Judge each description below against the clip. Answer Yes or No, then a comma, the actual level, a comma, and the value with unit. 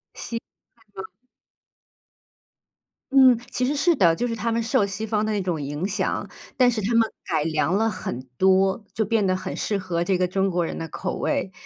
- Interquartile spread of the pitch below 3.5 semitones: No, average, 3.9 semitones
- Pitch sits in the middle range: No, high, 195 Hz